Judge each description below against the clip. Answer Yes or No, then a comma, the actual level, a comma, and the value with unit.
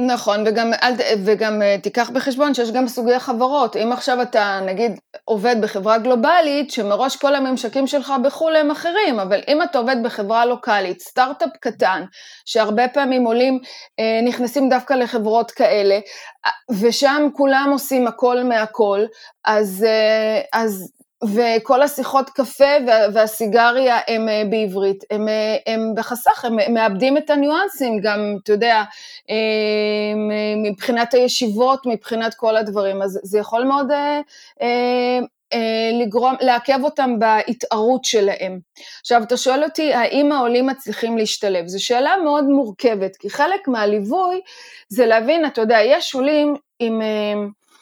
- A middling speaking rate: Yes, average, 125 wpm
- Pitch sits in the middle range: No, high, 240 Hz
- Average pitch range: Yes, average, 3.9 semitones